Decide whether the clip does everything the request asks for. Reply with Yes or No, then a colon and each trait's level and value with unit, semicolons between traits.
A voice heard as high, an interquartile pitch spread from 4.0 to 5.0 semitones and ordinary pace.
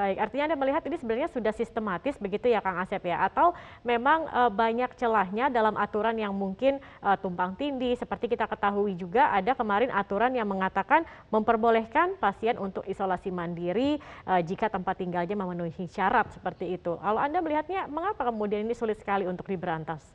No: high, 210 Hz; average, 4.4 semitones; fast, 160 wpm